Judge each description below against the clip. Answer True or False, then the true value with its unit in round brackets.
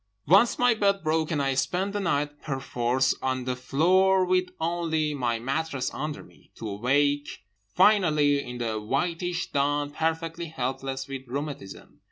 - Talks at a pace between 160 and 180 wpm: False (150 wpm)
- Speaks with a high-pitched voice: False (145 Hz)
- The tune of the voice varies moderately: True (4.3 semitones)